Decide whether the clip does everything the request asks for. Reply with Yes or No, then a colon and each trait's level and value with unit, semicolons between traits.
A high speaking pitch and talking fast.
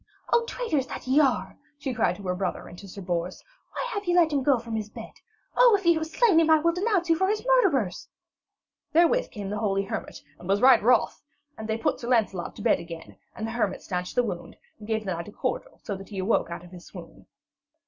Yes: high, 230 Hz; fast, 245 wpm